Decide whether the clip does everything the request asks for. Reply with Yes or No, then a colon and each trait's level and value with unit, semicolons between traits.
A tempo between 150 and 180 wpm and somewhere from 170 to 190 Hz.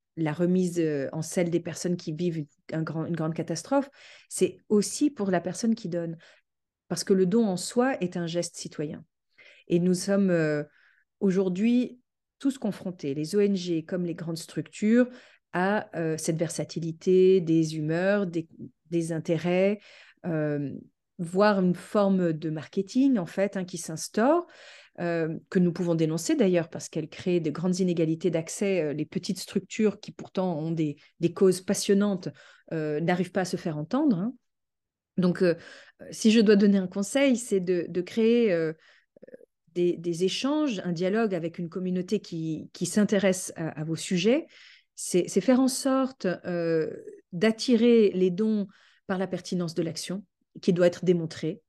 Yes: average, 160 wpm; medium, 185 Hz